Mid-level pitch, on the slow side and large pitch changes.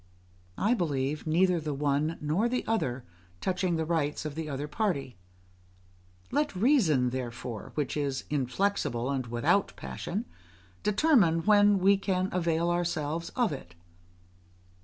Yes: medium, 160 Hz; slow, 130 wpm; wide, 5.7 semitones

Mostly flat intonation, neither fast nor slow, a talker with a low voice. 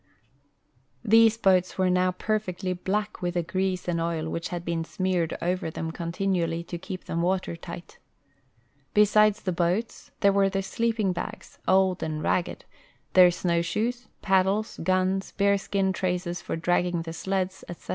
No: narrow, 2.1 semitones; average, 155 wpm; medium, 185 Hz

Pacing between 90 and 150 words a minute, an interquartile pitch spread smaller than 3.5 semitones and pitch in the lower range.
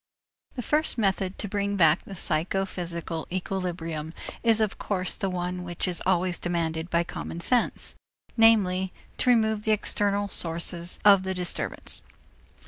No: average, 140 wpm; average, 2.9 semitones; medium, 185 Hz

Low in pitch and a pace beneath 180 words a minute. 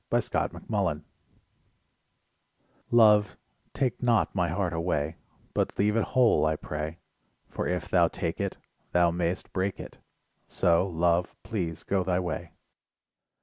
Yes: very low, 90 Hz; average, 140 wpm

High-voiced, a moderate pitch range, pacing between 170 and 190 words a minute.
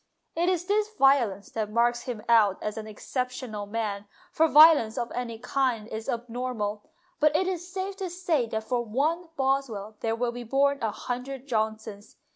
Yes: high, 245 Hz; average, 4.4 semitones; average, 175 wpm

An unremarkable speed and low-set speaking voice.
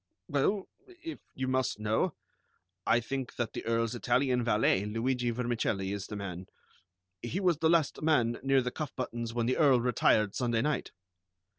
Yes: average, 165 wpm; low, 120 Hz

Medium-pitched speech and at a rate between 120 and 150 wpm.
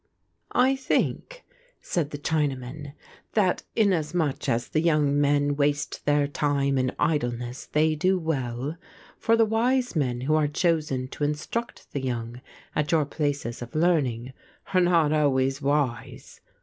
Yes: medium, 145 Hz; average, 140 wpm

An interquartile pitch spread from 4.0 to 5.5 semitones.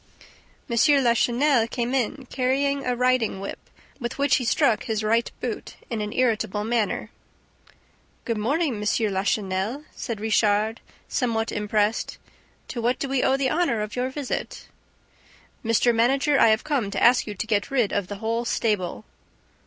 No: average, 3.2 semitones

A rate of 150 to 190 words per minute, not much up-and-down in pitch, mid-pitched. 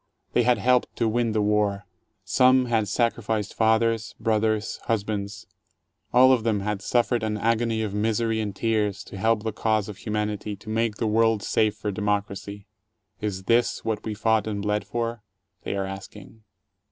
No: average, 175 wpm; narrow, 1.7 semitones; low, 110 Hz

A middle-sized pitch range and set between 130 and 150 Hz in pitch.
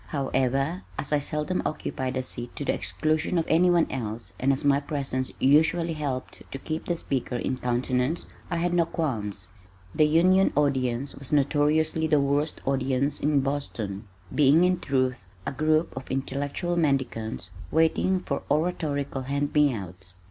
Yes: average, 3.3 semitones; medium, 140 Hz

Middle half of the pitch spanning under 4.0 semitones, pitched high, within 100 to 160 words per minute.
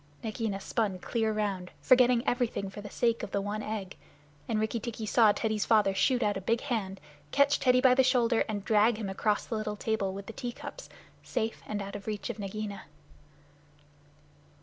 No: narrow, 2.6 semitones; high, 215 Hz; average, 190 wpm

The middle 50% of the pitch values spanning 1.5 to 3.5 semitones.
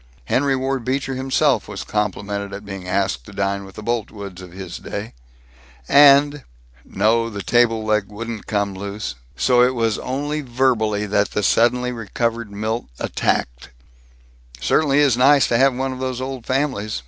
No: average, 4.3 semitones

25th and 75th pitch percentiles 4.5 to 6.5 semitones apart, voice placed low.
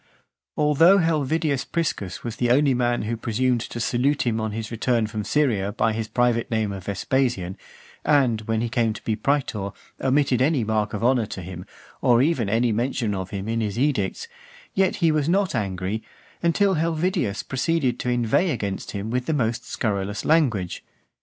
Yes: average, 5.0 semitones; low, 120 Hz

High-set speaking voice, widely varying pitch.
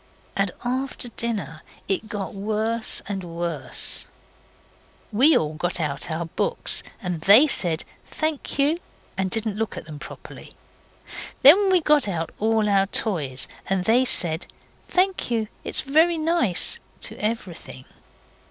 Yes: high, 210 Hz; wide, 6.9 semitones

